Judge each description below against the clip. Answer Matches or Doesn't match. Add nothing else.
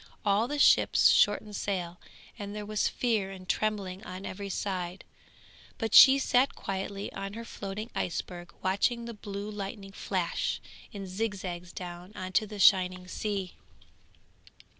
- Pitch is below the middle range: Doesn't match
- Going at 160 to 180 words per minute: Doesn't match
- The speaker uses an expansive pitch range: Doesn't match